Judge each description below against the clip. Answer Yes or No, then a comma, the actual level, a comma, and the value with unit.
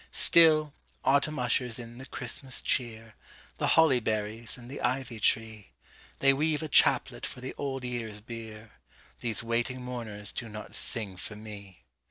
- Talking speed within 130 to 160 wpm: Yes, average, 140 wpm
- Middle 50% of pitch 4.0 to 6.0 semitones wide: No, average, 3.3 semitones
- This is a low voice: Yes, low, 120 Hz